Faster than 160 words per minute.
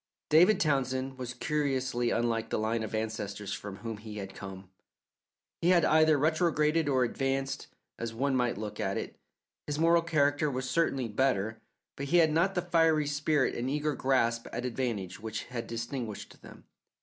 Yes: average, 170 wpm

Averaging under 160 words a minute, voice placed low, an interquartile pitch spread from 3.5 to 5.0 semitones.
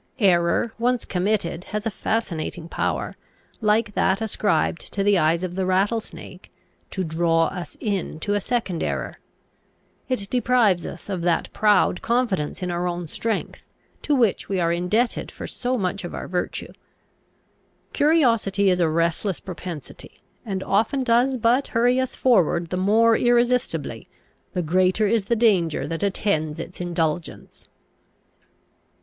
No: average, 145 wpm; high, 195 Hz; average, 4.7 semitones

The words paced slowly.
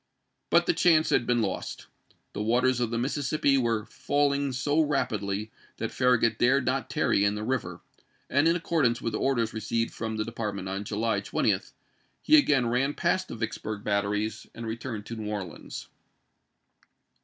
No: average, 165 wpm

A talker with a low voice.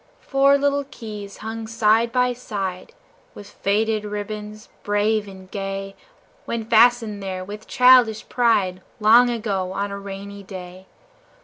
No: high, 210 Hz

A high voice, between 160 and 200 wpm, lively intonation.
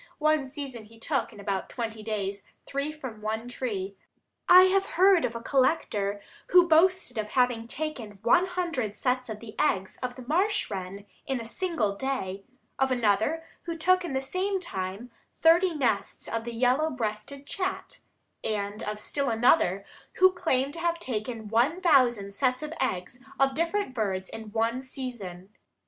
Yes: very high, 250 Hz; average, 165 wpm; wide, 6.7 semitones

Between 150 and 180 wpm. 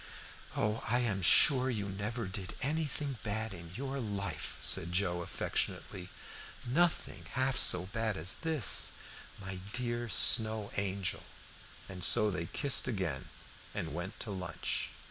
No: slow, 135 wpm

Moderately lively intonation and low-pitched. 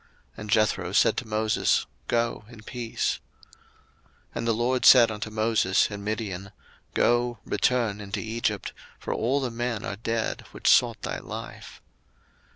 No: narrow, 2.1 semitones; low, 110 Hz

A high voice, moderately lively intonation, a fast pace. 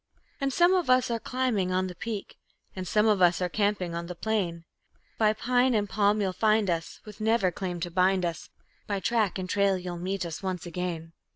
Yes: high, 195 Hz; average, 3.4 semitones; fast, 210 wpm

